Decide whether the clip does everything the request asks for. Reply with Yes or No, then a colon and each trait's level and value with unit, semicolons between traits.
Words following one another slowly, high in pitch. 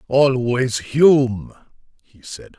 No: slow, 95 wpm; low, 125 Hz